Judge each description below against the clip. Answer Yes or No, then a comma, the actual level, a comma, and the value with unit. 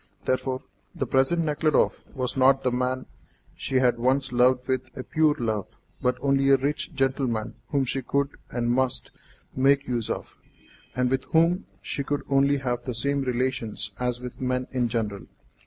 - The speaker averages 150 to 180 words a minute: Yes, average, 170 wpm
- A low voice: Yes, low, 130 Hz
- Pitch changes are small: Yes, narrow, 1.9 semitones